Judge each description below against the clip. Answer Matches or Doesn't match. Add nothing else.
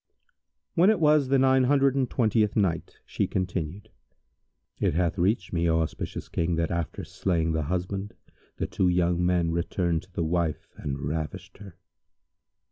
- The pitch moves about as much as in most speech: Matches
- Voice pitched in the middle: Doesn't match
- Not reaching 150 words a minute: Doesn't match